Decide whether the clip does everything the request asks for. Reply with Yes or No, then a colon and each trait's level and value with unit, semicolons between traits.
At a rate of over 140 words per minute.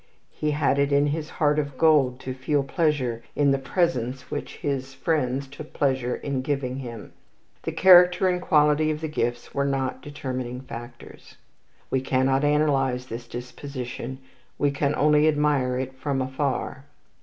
Yes: average, 155 wpm